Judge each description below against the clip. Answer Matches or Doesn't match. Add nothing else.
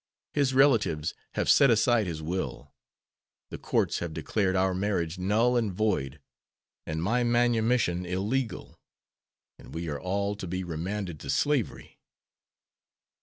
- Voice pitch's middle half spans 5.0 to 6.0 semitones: Matches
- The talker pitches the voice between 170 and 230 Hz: Doesn't match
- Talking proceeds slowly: Matches